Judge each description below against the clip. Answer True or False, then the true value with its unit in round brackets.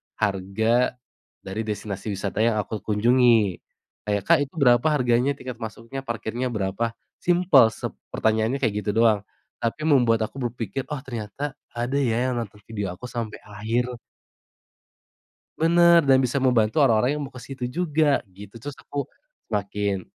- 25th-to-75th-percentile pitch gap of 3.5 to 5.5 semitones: True (4.1 semitones)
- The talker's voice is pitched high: False (115 Hz)